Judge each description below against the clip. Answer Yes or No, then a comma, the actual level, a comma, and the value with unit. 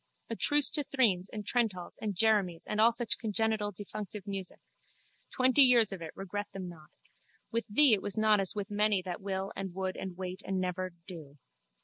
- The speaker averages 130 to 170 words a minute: No, average, 190 wpm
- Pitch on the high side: Yes, high, 200 Hz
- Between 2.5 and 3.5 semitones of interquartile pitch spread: Yes, average, 2.9 semitones